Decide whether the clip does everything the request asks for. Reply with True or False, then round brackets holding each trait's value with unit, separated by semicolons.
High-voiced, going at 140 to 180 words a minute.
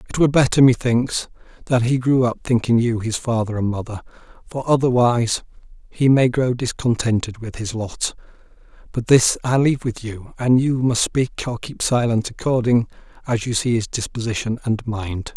False (120 Hz; 170 wpm)